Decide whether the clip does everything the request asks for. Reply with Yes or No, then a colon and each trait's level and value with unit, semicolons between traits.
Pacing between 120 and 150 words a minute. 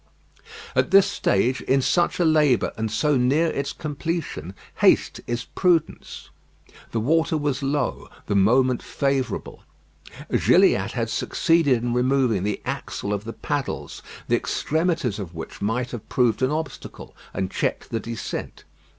Yes: average, 140 wpm